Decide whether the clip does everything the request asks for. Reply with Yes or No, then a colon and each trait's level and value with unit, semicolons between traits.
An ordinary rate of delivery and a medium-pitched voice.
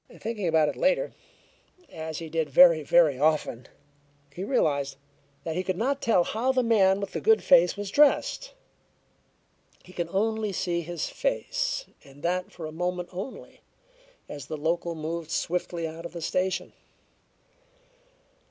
Yes: average, 150 wpm; medium, 175 Hz